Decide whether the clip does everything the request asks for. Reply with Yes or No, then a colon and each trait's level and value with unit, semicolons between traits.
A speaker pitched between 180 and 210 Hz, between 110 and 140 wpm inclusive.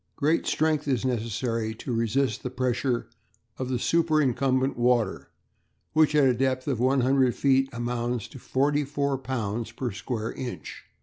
No: low, 130 Hz; slow, 135 wpm